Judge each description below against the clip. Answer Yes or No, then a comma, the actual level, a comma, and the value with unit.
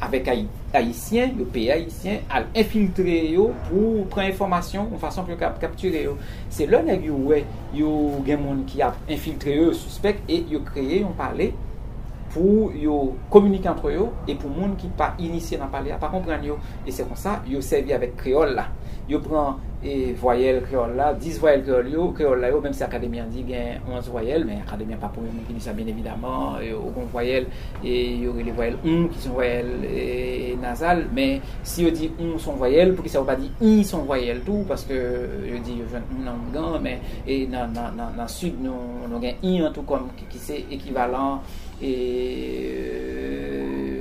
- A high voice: No, low, 130 Hz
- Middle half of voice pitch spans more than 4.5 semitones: Yes, average, 5.0 semitones